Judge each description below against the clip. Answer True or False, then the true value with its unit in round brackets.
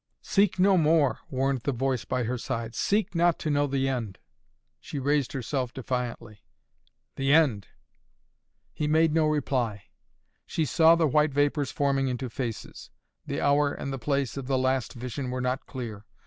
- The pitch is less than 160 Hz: True (135 Hz)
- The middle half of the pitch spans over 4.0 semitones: False (3.0 semitones)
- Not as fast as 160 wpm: False (165 wpm)